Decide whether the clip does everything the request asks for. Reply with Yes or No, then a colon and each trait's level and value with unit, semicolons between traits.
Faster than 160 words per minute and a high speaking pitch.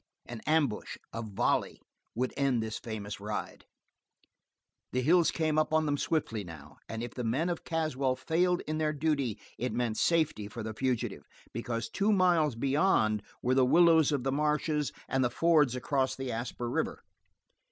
No: average, 170 wpm; low, 135 Hz